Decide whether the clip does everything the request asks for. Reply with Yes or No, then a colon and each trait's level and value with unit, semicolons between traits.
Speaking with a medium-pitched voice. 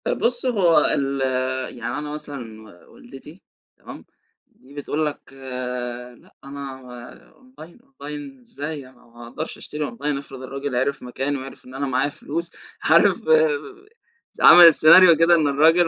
Yes: medium, 145 Hz